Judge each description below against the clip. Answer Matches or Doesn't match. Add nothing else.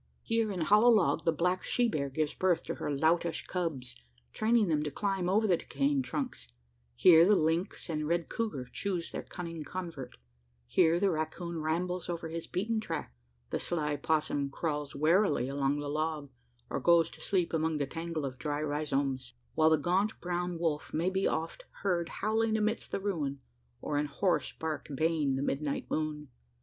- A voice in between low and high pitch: Matches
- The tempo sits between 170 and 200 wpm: Matches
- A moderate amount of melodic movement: Matches